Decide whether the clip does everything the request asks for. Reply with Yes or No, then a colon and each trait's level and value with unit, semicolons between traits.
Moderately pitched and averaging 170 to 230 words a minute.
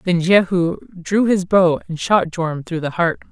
Yes: medium, 175 Hz; average, 200 wpm